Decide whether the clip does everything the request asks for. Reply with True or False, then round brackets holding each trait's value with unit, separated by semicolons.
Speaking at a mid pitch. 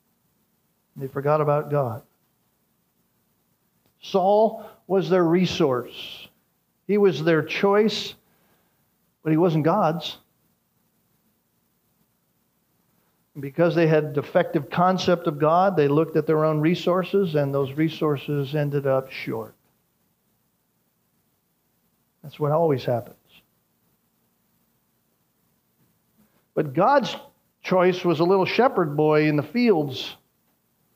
True (160 Hz)